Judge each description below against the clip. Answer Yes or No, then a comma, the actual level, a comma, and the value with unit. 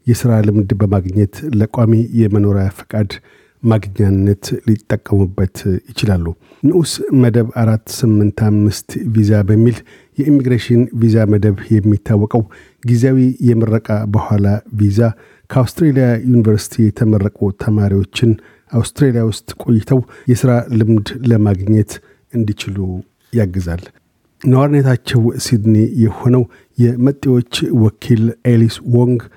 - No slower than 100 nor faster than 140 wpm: No, average, 90 wpm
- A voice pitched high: No, low, 110 Hz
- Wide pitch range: No, narrow, 2.6 semitones